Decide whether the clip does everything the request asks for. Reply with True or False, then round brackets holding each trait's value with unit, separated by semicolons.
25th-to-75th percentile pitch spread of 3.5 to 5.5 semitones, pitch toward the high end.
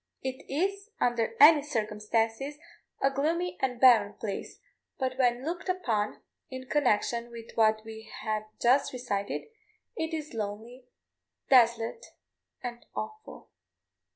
True (4.2 semitones; 245 Hz)